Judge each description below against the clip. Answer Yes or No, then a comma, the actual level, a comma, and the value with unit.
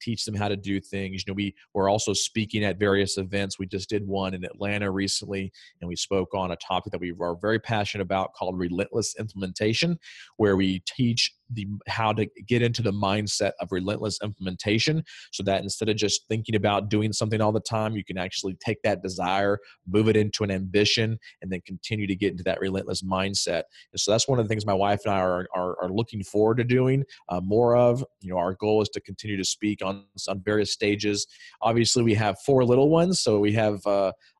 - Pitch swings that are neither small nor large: No, narrow, 2.1 semitones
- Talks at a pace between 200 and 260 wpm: Yes, fast, 220 wpm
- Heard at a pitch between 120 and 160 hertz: No, low, 100 Hz